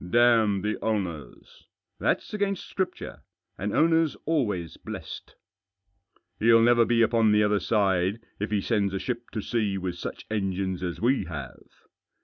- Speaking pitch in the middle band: No, low, 105 Hz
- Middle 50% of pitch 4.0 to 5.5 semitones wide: No, average, 3.4 semitones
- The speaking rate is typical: Yes, average, 160 wpm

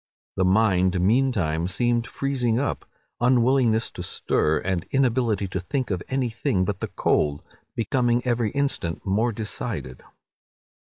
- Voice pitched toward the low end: Yes, low, 110 Hz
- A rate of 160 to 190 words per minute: No, slow, 135 wpm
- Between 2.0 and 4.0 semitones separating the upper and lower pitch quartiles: No, average, 4.9 semitones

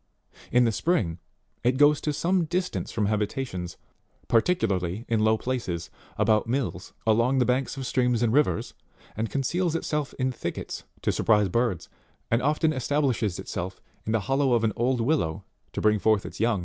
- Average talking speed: Yes, average, 170 wpm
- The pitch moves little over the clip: No, average, 4.4 semitones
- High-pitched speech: No, low, 120 Hz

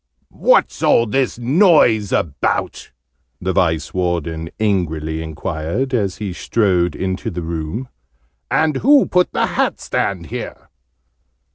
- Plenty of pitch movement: Yes, wide, 6.7 semitones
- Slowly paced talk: Yes, slow, 120 wpm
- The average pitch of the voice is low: Yes, very low, 95 Hz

